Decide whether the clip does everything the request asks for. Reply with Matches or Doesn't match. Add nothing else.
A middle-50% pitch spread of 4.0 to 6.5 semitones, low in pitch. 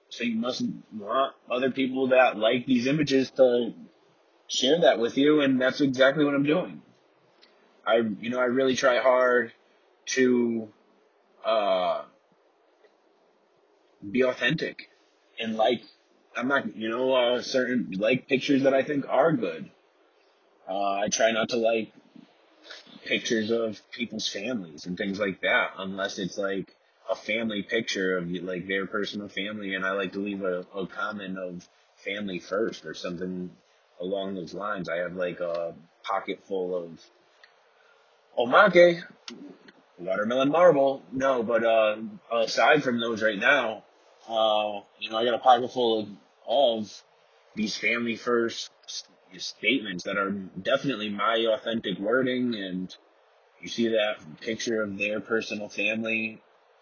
Matches